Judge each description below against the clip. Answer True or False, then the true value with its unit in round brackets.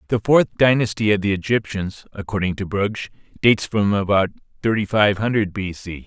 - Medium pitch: False (105 Hz)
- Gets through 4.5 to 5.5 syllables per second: True (5.1 syllables/s)